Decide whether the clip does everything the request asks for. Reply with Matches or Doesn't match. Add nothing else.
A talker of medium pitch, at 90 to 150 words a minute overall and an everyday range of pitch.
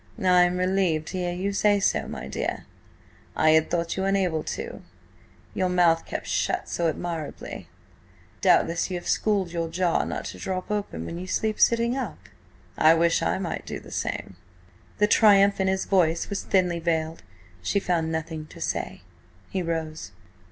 Doesn't match